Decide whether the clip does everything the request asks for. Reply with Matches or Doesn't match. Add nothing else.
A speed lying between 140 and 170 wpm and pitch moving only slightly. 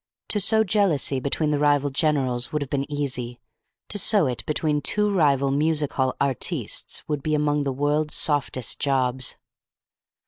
Matches